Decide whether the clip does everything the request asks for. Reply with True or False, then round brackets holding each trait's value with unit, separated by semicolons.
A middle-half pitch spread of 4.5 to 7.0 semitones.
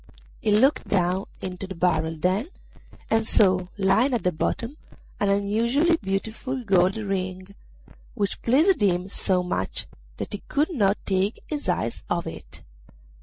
False (3.9 semitones)